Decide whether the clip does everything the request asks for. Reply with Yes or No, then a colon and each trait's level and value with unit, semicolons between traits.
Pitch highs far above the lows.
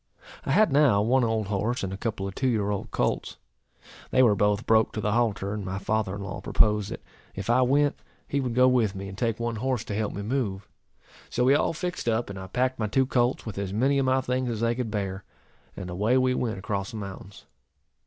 No: average, 4.1 semitones